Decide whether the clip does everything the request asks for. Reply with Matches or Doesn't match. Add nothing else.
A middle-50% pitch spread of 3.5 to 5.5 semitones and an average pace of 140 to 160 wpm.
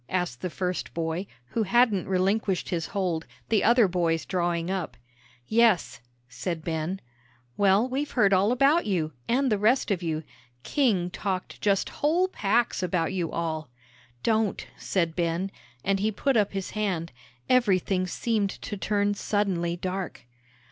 Matches